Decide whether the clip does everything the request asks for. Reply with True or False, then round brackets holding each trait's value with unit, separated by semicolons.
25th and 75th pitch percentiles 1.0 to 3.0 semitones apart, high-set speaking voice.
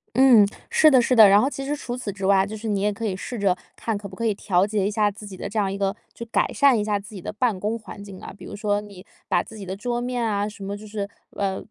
True (2.4 semitones; 210 Hz)